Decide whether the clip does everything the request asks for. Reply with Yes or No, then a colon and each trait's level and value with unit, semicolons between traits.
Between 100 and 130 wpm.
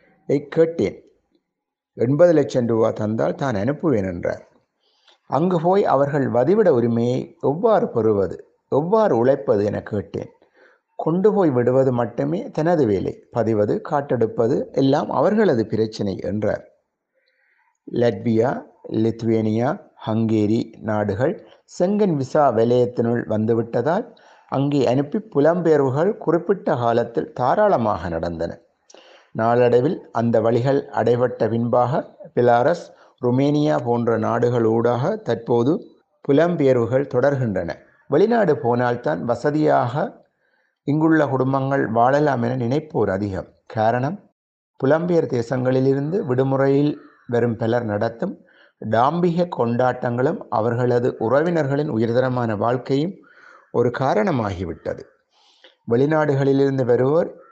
No: average, 90 wpm